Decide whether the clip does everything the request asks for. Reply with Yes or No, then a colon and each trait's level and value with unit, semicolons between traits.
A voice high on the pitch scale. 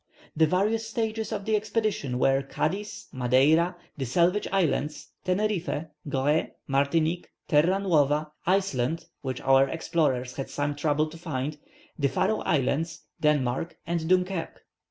No: medium, 160 Hz